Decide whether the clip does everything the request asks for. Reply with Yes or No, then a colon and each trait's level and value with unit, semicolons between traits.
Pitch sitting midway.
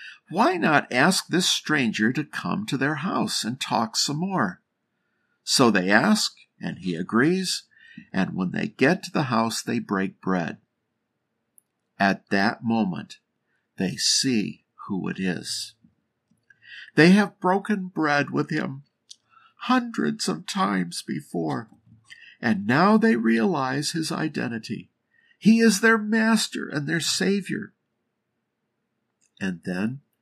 Yes: medium, 165 Hz